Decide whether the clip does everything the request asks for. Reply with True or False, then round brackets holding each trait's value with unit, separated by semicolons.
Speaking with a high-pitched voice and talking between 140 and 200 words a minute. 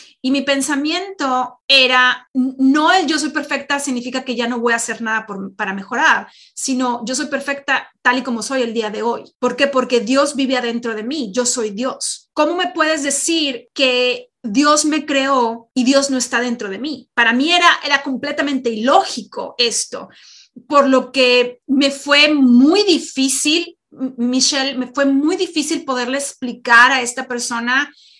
True (265 Hz; 175 wpm)